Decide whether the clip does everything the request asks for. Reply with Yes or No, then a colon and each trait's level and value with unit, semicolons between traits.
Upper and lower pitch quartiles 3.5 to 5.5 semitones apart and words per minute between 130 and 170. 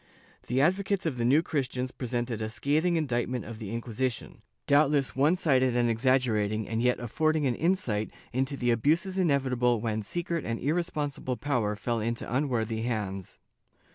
Yes: average, 4.2 semitones; average, 155 wpm